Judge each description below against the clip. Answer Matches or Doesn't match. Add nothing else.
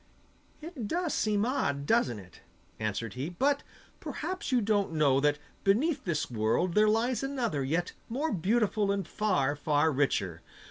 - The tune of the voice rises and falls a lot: Matches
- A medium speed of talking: Matches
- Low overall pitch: Doesn't match